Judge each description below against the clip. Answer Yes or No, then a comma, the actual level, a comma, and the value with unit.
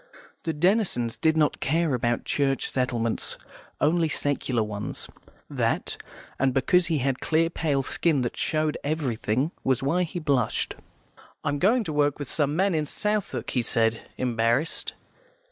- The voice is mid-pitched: Yes, medium, 145 Hz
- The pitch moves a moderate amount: Yes, average, 4.5 semitones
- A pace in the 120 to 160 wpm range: Yes, average, 150 wpm